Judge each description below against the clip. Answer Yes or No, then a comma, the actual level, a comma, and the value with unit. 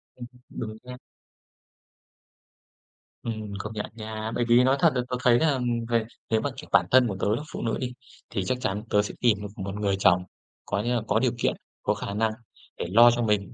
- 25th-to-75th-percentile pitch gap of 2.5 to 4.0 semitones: Yes, average, 3.0 semitones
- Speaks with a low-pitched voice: Yes, low, 110 Hz